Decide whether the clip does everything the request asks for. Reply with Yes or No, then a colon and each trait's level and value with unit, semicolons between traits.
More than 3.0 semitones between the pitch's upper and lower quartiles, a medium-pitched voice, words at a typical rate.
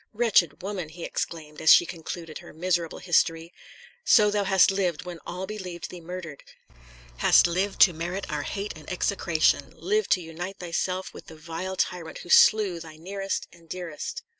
No: average, 2.7 semitones; medium, 175 Hz; average, 170 wpm